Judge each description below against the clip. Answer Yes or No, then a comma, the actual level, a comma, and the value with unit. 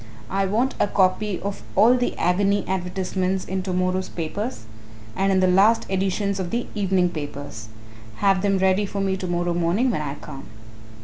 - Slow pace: No, average, 175 wpm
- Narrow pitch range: Yes, narrow, 2.0 semitones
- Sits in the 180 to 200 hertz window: Yes, high, 190 Hz